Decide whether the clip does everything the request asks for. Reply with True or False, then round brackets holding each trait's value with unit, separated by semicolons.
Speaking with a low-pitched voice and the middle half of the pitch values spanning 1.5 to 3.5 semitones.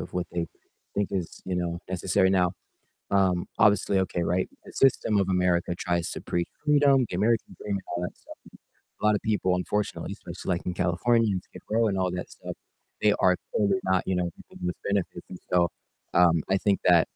True (95 Hz; 2.4 semitones)